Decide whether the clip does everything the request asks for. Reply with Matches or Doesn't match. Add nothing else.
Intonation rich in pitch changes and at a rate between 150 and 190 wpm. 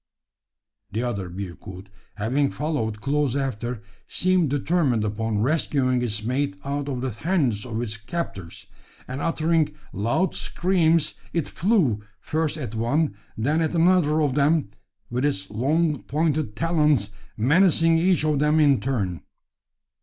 Doesn't match